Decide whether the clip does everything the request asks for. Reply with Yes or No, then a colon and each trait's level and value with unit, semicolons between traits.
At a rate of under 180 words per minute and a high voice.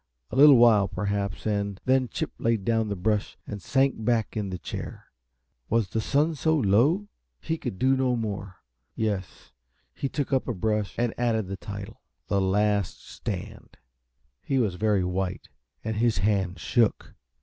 No: average, 165 wpm; low, 110 Hz